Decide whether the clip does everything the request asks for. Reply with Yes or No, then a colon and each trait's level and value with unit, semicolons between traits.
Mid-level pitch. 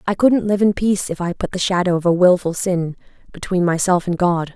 Yes: medium, 180 Hz